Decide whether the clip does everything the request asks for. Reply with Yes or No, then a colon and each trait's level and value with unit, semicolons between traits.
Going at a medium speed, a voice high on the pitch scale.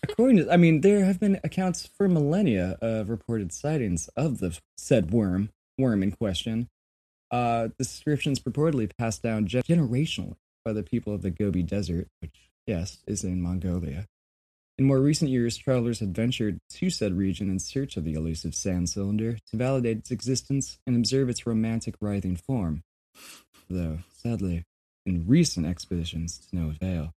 No: average, 160 wpm; low, 105 Hz